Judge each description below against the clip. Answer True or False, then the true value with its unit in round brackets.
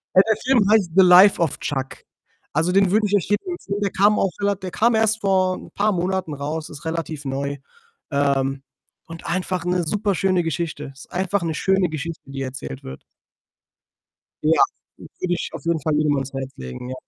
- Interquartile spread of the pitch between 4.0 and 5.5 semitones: True (5.1 semitones)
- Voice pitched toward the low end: False (175 Hz)